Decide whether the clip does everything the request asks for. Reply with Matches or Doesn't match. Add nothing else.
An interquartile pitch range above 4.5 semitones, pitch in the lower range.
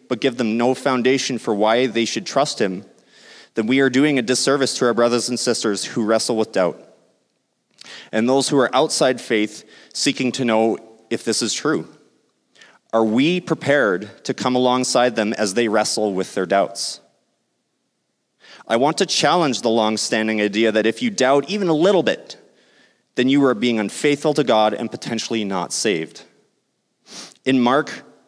Doesn't match